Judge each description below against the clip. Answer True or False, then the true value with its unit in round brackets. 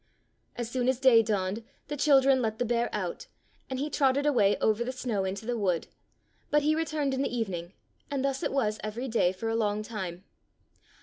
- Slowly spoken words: False (200 wpm)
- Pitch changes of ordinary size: True (4.2 semitones)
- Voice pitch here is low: False (235 Hz)